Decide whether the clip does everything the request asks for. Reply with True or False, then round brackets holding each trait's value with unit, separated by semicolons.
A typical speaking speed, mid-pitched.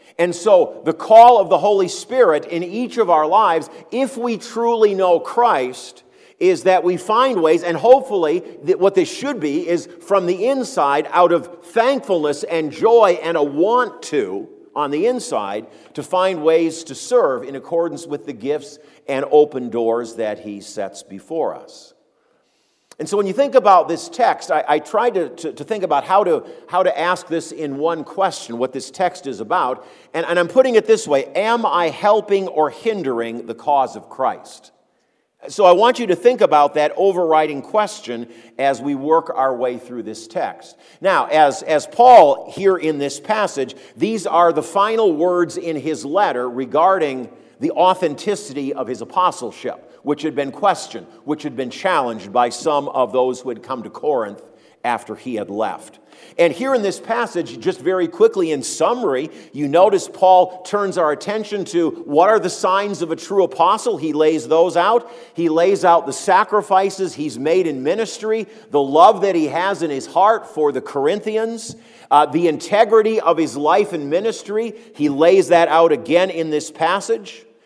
True (180 wpm; 175 Hz)